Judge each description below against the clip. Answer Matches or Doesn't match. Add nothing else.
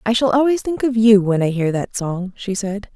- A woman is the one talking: Matches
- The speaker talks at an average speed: Doesn't match